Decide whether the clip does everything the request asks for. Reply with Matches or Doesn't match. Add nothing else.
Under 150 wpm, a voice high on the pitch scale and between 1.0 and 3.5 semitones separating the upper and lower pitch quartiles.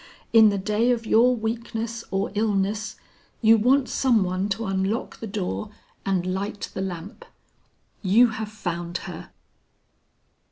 Matches